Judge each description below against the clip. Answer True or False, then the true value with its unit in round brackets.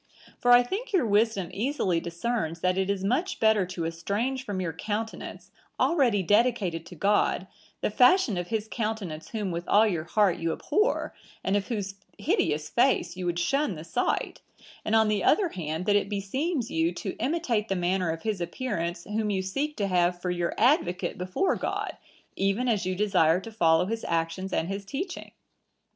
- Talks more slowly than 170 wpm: False (185 wpm)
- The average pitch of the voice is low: False (200 Hz)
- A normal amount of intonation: True (4.9 semitones)